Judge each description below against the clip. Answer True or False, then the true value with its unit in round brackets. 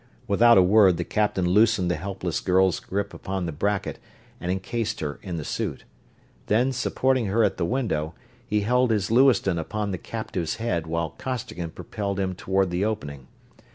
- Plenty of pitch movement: False (4.0 semitones)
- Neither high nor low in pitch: False (95 Hz)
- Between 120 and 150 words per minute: False (175 wpm)